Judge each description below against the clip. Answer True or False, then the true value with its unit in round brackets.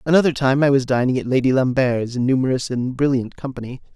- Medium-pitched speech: False (130 Hz)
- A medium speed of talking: True (195 wpm)